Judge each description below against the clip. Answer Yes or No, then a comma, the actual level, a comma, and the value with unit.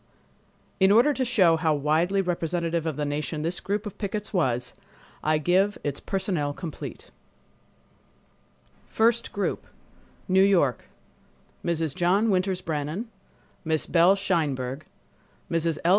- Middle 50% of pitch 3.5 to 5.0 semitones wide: Yes, average, 4.2 semitones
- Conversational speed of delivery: No, slow, 120 wpm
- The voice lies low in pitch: No, medium, 170 Hz